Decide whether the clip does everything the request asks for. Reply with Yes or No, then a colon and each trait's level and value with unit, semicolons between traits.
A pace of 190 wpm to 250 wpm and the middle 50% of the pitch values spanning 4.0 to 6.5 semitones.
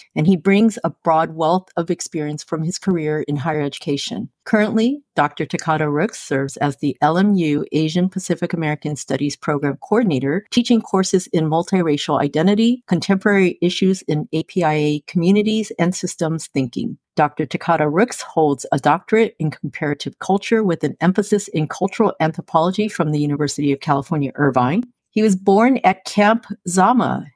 No: average, 150 wpm; average, 4.6 semitones